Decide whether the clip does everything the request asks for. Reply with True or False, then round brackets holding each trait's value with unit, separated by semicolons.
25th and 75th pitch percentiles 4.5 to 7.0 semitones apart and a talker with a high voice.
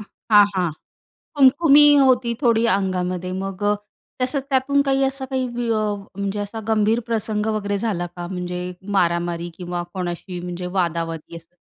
True (5.0 semitones; 200 Hz)